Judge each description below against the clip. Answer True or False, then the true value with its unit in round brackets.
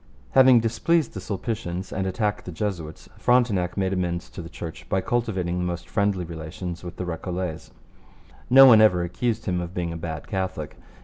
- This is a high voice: False (90 Hz)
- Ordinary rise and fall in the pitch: True (3.7 semitones)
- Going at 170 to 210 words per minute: True (180 wpm)